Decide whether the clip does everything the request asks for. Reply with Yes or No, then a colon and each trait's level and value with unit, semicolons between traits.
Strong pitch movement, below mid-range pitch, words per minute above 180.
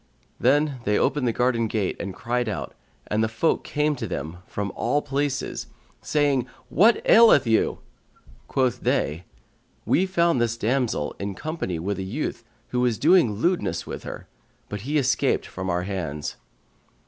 No: wide, 6.4 semitones; low, 120 Hz; average, 160 wpm